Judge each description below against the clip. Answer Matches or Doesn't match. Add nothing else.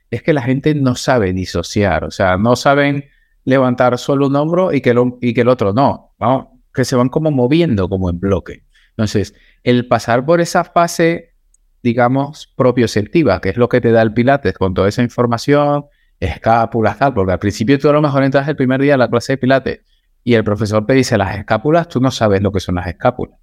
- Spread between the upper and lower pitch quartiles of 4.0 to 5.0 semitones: Matches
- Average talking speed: Doesn't match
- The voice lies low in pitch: Matches